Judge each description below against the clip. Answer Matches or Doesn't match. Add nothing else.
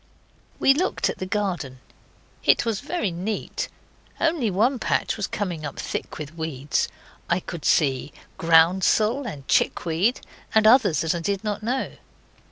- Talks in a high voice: Matches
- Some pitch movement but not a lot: Doesn't match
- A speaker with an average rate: Matches